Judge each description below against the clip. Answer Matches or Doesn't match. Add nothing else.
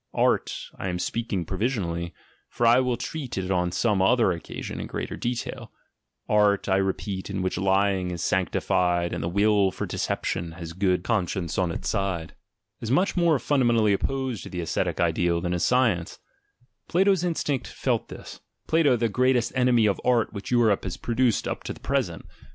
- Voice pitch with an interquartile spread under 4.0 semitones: Doesn't match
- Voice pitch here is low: Matches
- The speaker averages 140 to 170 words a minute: Doesn't match